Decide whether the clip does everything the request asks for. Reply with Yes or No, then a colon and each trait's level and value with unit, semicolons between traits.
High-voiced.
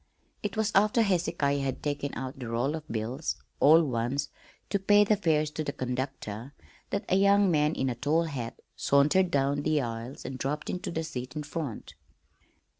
No: medium, 145 Hz